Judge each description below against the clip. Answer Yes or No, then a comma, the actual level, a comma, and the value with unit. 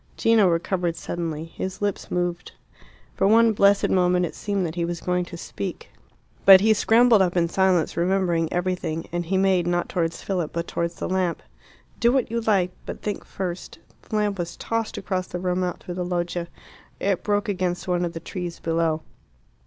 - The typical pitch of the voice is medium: Yes, medium, 180 Hz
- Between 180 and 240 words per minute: Yes, average, 190 wpm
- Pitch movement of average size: No, narrow, 2.3 semitones